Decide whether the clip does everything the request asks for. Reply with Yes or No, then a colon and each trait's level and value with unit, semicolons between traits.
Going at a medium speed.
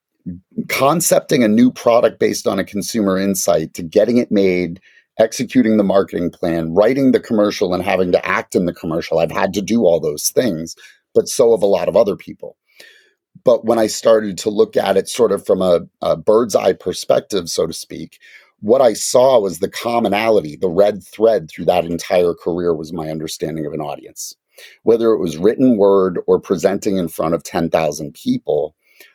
Yes: average, 190 wpm